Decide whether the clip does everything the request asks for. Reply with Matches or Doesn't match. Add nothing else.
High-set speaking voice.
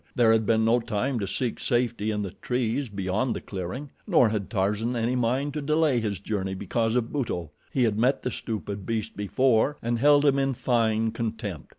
Doesn't match